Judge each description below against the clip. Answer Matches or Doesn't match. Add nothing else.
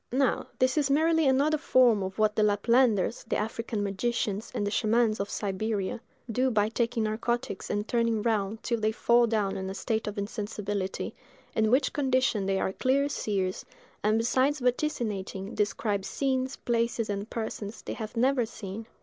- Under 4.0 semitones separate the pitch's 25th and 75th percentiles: Matches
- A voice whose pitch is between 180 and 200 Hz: Doesn't match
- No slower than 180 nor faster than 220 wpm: Doesn't match